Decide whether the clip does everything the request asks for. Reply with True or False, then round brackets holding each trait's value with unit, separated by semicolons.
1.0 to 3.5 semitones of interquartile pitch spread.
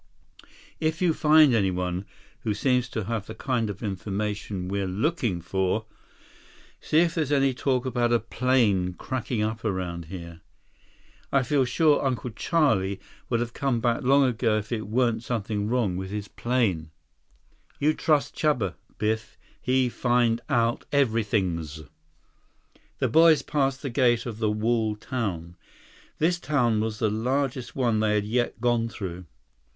False (4.1 semitones)